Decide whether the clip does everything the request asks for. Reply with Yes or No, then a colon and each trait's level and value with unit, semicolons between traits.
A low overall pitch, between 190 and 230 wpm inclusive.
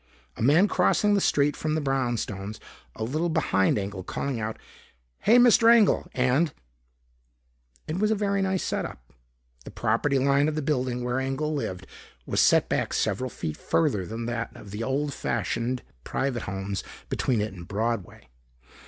No: low, 130 Hz; average, 165 wpm